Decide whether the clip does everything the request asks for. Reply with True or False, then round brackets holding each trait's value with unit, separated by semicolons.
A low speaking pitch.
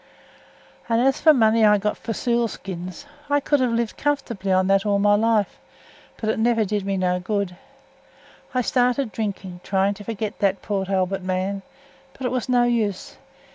False (210 Hz)